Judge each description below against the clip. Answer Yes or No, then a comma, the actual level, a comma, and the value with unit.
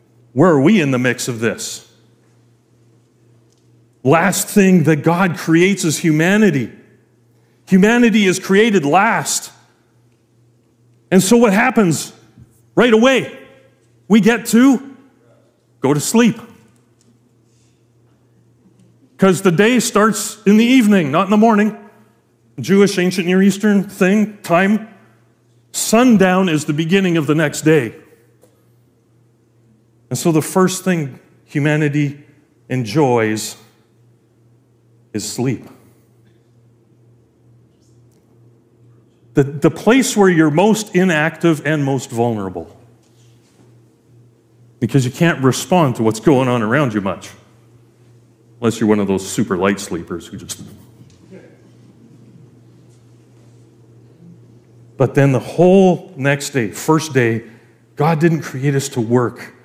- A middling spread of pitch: No, wide, 7.3 semitones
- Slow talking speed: Yes, slow, 110 wpm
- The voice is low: Yes, low, 125 Hz